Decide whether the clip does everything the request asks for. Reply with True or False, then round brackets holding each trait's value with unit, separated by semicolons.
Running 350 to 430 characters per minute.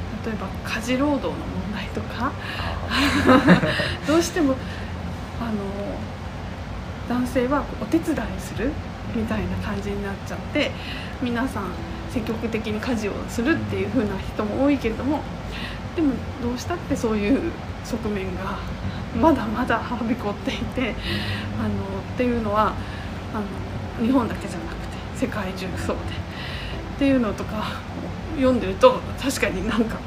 False (270 characters per minute)